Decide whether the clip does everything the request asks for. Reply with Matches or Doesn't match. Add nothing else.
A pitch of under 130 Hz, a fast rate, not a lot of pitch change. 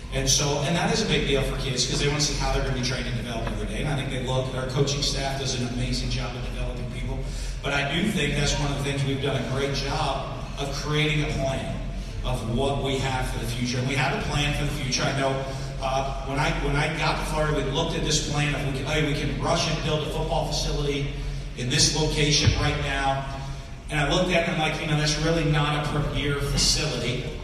Doesn't match